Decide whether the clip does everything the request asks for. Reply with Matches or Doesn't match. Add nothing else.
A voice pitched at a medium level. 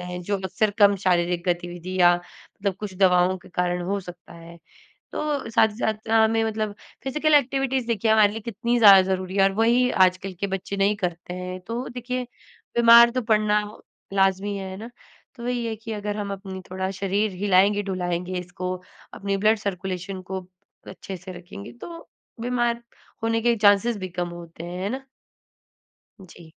Doesn't match